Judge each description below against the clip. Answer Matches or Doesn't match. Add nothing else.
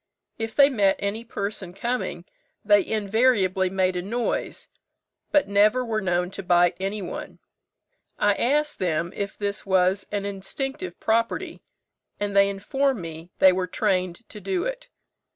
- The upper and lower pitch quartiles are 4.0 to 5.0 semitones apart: Doesn't match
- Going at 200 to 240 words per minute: Doesn't match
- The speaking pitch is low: Doesn't match